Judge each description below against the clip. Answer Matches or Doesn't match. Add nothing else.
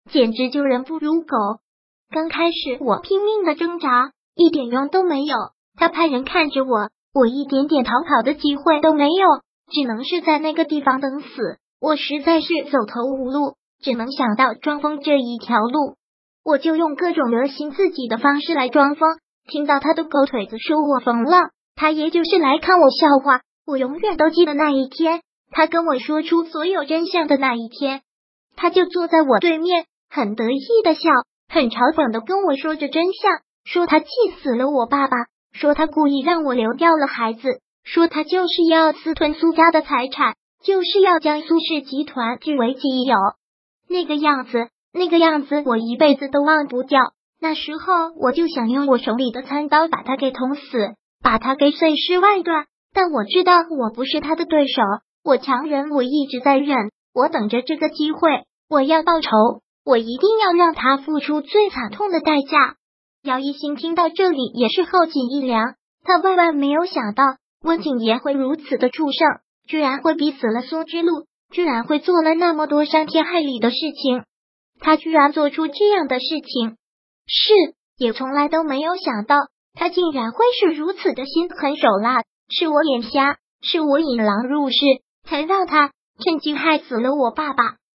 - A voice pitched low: Doesn't match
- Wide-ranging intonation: Doesn't match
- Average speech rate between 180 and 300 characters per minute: Matches